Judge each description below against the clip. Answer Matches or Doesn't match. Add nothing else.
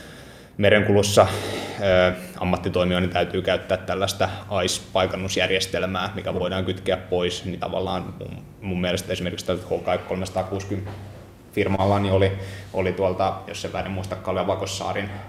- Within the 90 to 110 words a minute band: Matches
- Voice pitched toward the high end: Doesn't match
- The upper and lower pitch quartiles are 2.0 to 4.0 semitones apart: Doesn't match